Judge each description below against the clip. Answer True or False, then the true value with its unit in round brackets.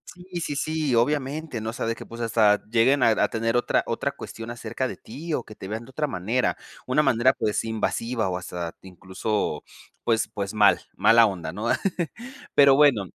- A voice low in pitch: True (115 Hz)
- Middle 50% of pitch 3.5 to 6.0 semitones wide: True (4.0 semitones)